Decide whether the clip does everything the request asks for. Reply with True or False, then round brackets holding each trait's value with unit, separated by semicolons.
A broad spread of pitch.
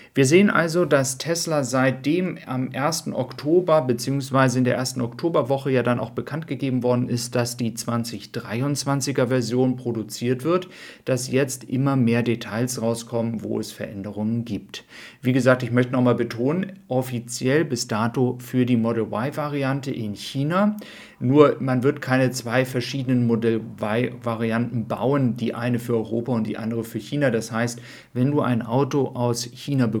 False (2.7 semitones)